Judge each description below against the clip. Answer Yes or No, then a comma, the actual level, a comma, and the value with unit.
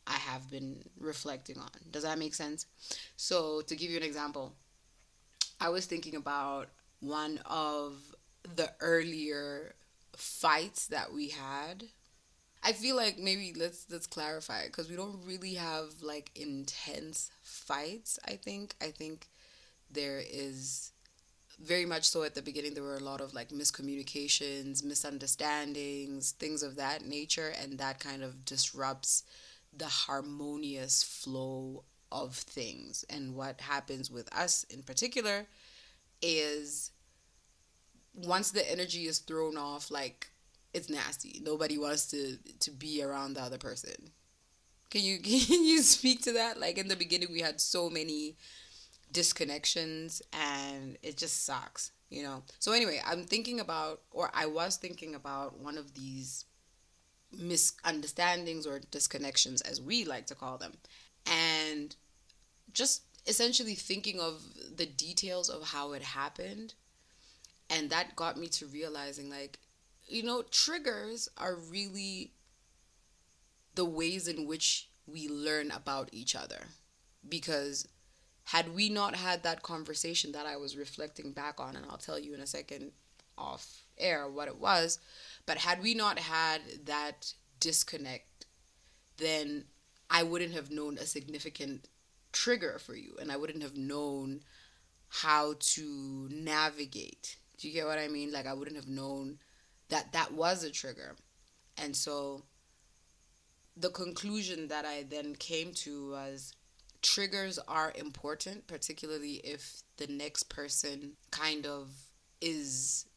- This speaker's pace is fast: No, average, 140 wpm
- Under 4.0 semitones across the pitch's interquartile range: Yes, average, 3.3 semitones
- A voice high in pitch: No, medium, 150 Hz